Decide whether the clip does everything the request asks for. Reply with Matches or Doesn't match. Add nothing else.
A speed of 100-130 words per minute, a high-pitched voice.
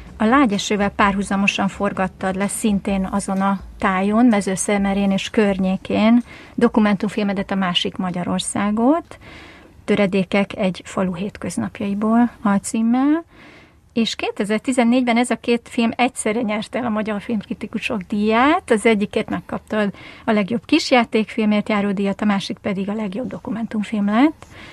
Matches